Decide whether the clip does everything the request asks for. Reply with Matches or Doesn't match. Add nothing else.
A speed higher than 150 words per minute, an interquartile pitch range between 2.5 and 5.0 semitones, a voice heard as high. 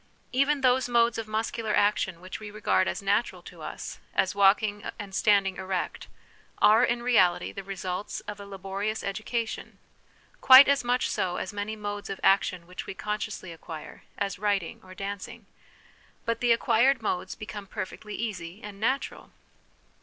Matches